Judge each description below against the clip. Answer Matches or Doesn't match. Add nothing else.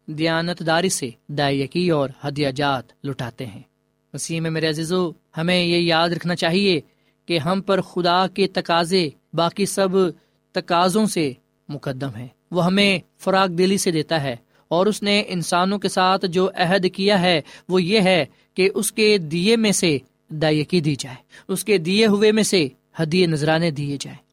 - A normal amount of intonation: Matches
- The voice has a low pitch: Doesn't match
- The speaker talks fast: Doesn't match